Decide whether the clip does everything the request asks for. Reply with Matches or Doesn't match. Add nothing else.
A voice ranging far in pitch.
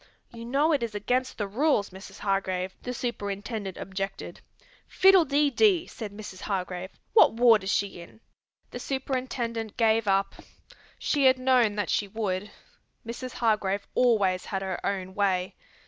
Doesn't match